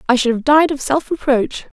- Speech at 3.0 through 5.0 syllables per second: No, 5.3 syllables/s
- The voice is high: Yes, very high, 270 Hz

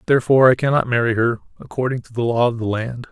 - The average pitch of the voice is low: Yes, low, 120 Hz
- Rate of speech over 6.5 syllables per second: Yes, 7.0 syllables/s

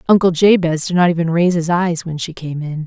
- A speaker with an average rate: No, fast, 250 wpm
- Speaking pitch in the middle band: Yes, medium, 170 Hz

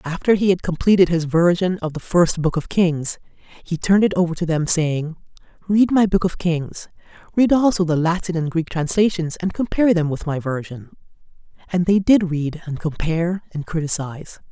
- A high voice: No, medium, 170 Hz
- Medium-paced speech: Yes, average, 180 wpm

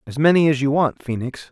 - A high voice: No, medium, 140 Hz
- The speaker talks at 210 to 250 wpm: Yes, fast, 235 wpm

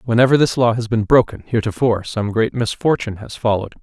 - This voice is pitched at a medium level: No, low, 115 Hz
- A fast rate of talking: No, average, 190 wpm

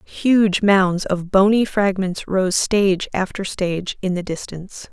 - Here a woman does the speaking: Yes, female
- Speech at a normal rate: Yes, average, 145 wpm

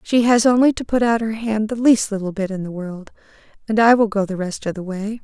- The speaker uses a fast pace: Yes, fast, 275 wpm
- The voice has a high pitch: Yes, high, 215 Hz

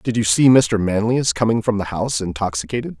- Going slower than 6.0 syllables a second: Yes, 5.8 syllables/s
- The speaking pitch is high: No, low, 105 Hz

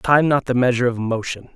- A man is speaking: Yes, male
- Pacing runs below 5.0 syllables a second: No, 6.0 syllables/s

